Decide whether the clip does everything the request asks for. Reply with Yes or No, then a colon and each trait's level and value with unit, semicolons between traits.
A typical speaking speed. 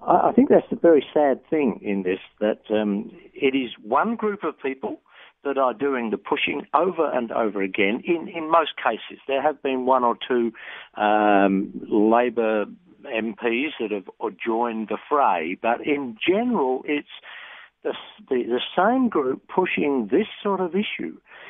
Yes: average, 160 wpm